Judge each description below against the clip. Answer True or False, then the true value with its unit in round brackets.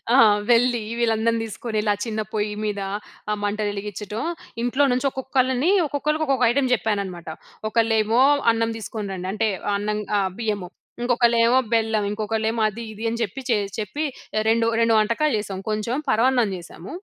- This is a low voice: False (225 Hz)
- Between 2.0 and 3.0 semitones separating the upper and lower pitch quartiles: True (2.4 semitones)